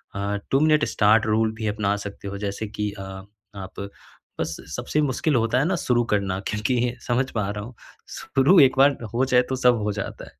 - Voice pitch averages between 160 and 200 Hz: No, low, 110 Hz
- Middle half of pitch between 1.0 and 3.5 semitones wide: No, average, 4.2 semitones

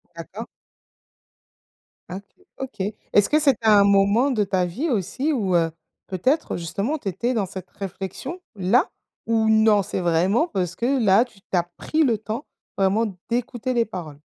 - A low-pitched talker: No, high, 210 Hz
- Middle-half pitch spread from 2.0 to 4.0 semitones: No, average, 4.6 semitones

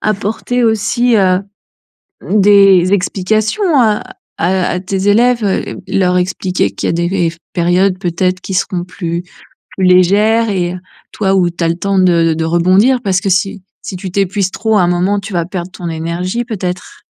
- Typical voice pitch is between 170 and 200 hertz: Yes, high, 190 Hz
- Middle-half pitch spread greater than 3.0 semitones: No, narrow, 2.5 semitones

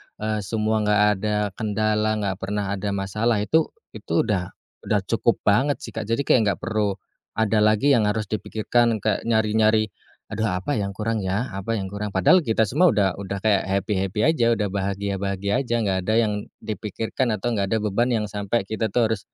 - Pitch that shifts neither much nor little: No, narrow, 2.1 semitones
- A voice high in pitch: No, low, 105 Hz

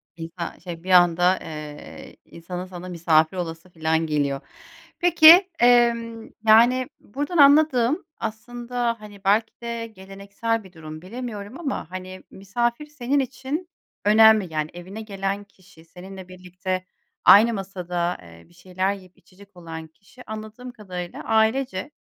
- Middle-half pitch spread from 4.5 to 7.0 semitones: Yes, average, 4.9 semitones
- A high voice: Yes, high, 195 Hz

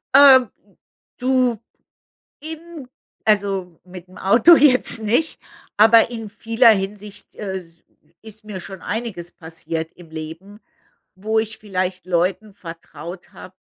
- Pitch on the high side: Yes, high, 205 Hz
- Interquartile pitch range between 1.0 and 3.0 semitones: No, average, 4.1 semitones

